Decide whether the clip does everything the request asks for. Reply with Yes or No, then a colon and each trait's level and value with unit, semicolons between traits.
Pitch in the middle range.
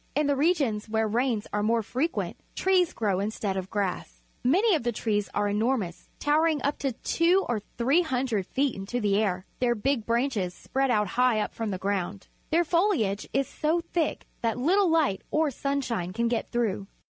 No: high, 235 Hz